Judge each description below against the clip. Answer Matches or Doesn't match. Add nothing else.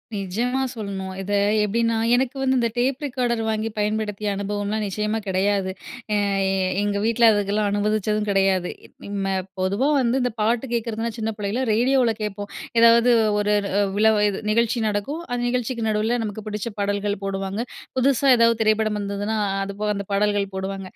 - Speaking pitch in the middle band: Doesn't match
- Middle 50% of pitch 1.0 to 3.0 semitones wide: Matches